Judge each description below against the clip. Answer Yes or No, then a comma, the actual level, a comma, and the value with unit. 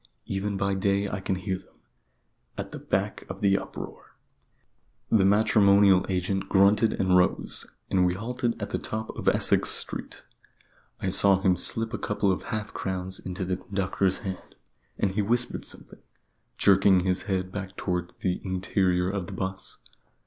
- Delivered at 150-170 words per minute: Yes, average, 165 wpm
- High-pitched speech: No, very low, 95 Hz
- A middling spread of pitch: No, narrow, 1.6 semitones